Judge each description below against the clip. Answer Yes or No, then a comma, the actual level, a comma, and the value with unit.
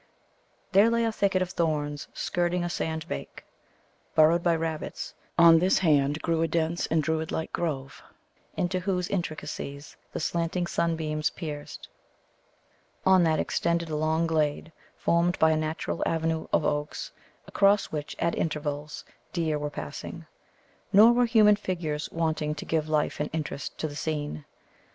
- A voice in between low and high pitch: Yes, medium, 160 Hz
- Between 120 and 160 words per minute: Yes, average, 150 wpm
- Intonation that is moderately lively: No, narrow, 2.3 semitones